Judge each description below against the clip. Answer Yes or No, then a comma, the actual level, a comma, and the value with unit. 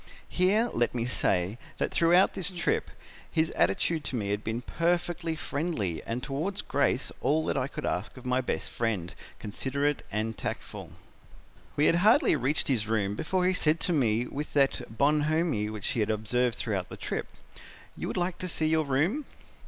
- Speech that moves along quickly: No, average, 180 wpm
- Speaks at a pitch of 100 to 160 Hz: Yes, medium, 140 Hz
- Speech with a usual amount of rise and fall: No, wide, 6.9 semitones